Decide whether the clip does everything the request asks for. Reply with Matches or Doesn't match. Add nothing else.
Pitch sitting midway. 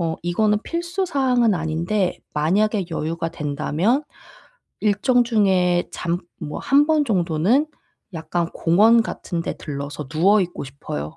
Matches